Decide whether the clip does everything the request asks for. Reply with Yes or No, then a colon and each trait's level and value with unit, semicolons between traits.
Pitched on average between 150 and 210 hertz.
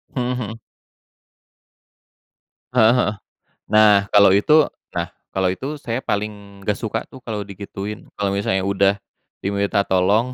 No: low, 105 Hz